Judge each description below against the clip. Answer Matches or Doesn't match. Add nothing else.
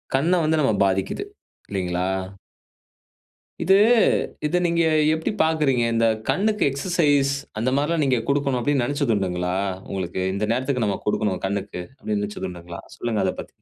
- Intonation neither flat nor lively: Doesn't match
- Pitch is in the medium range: Doesn't match